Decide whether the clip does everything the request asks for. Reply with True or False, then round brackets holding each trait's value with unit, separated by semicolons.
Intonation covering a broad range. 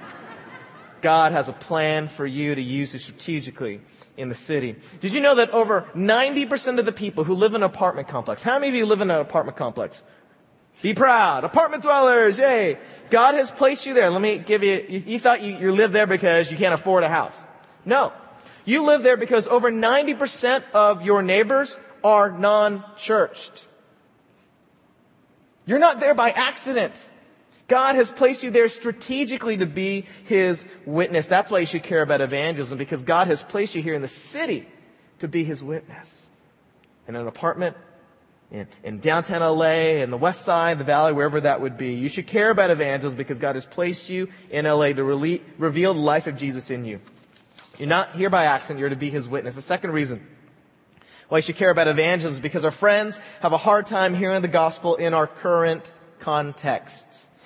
True (6.1 semitones)